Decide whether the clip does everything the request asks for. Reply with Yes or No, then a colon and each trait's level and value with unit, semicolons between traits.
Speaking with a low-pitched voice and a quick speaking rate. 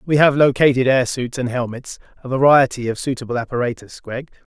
No: low, 130 Hz; average, 160 wpm